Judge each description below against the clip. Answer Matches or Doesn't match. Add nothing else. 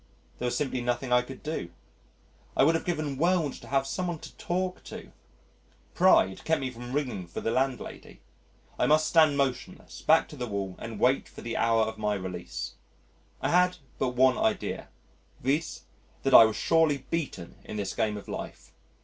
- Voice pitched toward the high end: Doesn't match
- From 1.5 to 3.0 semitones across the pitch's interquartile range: Doesn't match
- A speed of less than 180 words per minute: Doesn't match